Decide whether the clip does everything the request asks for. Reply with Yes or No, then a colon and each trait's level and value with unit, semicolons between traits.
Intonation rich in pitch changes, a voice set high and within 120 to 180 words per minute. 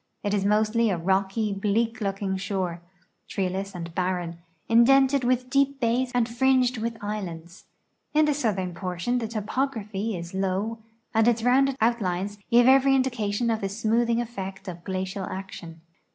No: average, 4.0 semitones; high, 215 Hz; average, 150 wpm